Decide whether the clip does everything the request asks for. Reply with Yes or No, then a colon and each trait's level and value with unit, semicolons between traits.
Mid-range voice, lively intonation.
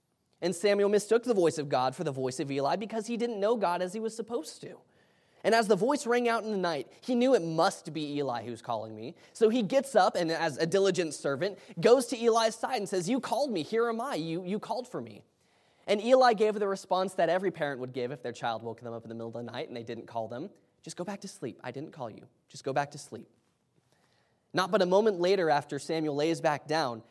Yes: medium, 175 Hz; wide, 7.5 semitones